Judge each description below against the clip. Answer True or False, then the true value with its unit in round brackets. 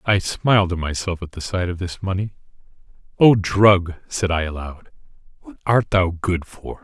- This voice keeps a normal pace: True (175 wpm)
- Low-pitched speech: True (90 Hz)